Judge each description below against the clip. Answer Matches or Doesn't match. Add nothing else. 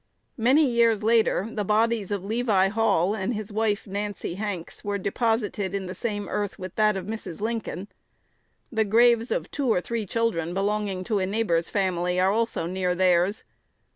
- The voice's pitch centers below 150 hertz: Doesn't match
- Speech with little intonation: Doesn't match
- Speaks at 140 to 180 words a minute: Matches